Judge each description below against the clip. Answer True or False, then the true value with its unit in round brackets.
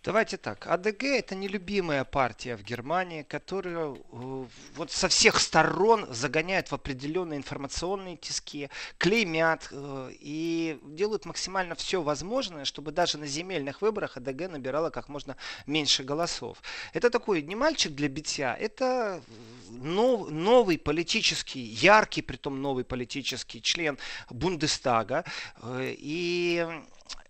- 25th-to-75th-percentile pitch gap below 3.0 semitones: False (5.1 semitones)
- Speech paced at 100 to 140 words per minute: True (110 wpm)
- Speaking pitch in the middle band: True (155 Hz)